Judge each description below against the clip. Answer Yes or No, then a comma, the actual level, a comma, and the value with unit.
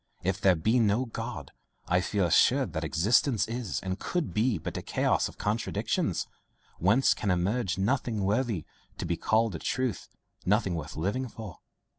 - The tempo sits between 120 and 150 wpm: No, average, 165 wpm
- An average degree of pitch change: Yes, average, 4.5 semitones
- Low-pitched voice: Yes, low, 105 Hz